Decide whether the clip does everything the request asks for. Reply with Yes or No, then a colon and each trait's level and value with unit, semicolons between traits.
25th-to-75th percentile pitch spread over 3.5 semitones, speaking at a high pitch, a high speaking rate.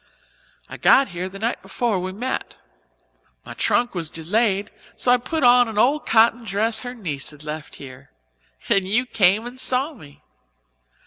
No: average, 5.0 semitones; high, 220 Hz; average, 170 wpm